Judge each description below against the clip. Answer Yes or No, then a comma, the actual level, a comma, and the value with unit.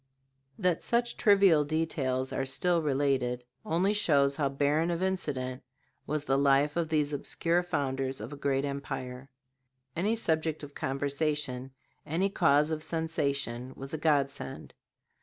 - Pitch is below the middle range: No, medium, 145 Hz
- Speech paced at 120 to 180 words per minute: Yes, average, 140 wpm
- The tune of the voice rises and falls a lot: No, average, 3.2 semitones